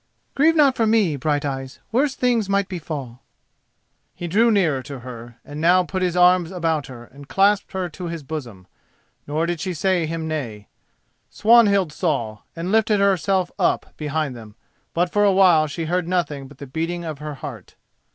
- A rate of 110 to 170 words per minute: No, average, 180 wpm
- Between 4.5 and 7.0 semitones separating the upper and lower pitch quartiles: Yes, average, 5.0 semitones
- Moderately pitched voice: Yes, medium, 165 Hz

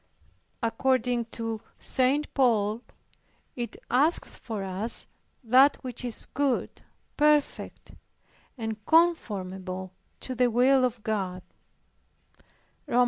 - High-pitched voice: Yes, high, 240 Hz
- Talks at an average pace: No, slow, 95 wpm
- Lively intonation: No, average, 3.5 semitones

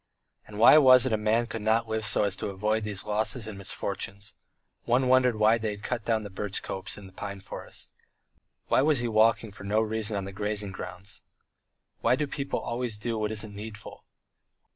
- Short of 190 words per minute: No, fast, 205 wpm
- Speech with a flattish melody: Yes, narrow, 2.2 semitones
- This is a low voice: Yes, low, 110 Hz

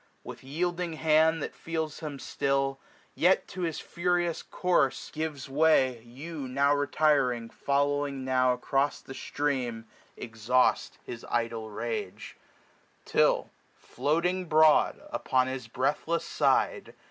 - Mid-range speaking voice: Yes, medium, 145 Hz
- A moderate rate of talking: No, slow, 125 wpm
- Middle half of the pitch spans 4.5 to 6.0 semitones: No, average, 3.7 semitones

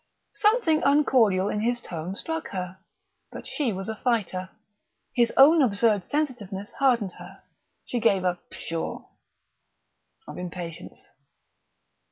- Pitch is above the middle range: Yes, high, 220 Hz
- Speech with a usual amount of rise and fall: No, wide, 6.3 semitones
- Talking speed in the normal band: No, slow, 120 wpm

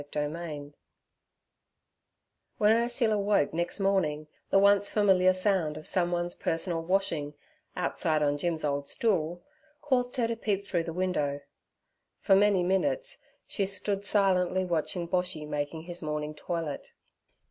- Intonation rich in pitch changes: No, average, 4.3 semitones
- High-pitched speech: No, medium, 180 Hz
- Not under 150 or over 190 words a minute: No, slow, 135 wpm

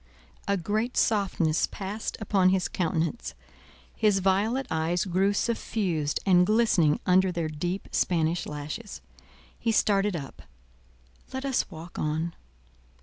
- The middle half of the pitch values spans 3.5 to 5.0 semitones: Yes, average, 4.0 semitones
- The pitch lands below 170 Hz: No, medium, 185 Hz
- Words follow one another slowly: Yes, slow, 120 wpm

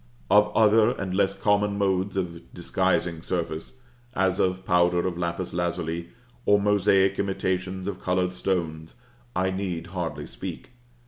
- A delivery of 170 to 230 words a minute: No, slow, 135 wpm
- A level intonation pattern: Yes, narrow, 2.1 semitones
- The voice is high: No, very low, 95 Hz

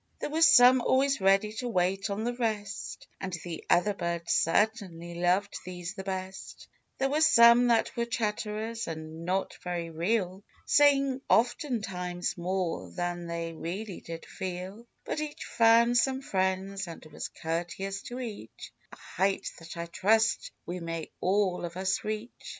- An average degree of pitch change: Yes, average, 4.7 semitones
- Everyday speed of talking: Yes, average, 155 wpm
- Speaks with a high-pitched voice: Yes, high, 195 Hz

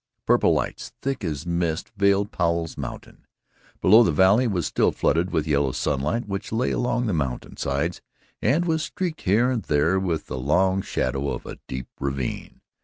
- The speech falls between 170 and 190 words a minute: Yes, average, 175 wpm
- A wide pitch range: Yes, wide, 6.8 semitones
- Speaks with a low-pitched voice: Yes, very low, 90 Hz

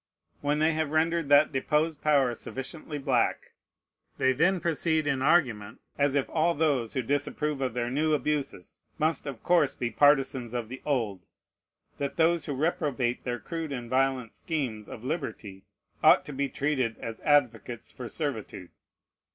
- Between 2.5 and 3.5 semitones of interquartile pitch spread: No, average, 3.9 semitones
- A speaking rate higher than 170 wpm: No, average, 160 wpm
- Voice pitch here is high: No, medium, 140 Hz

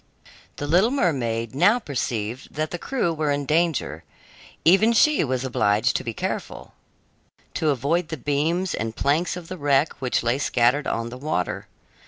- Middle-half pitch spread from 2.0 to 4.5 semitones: No, wide, 5.5 semitones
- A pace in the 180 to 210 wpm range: No, average, 165 wpm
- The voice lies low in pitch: No, medium, 145 Hz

